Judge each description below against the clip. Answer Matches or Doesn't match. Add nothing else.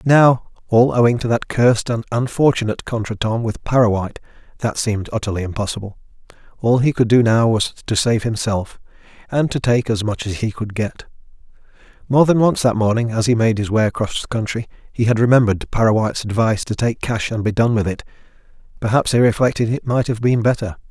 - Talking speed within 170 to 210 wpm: Matches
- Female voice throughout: Doesn't match